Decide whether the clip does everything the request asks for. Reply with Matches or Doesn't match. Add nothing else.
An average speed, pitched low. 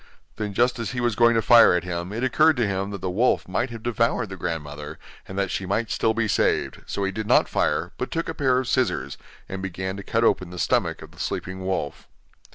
Doesn't match